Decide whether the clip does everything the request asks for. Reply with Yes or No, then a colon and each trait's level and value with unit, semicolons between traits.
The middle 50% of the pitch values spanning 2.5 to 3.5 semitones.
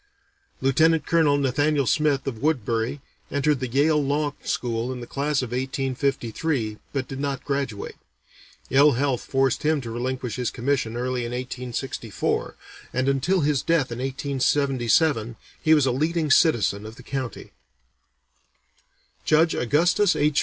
Yes: average, 3.0 semitones